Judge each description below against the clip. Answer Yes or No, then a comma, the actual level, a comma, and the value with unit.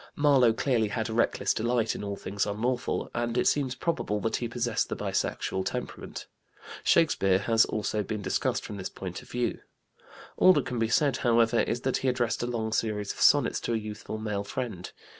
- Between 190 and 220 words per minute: Yes, average, 195 wpm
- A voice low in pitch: Yes, low, 115 Hz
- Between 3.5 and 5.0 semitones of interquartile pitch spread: No, average, 2.7 semitones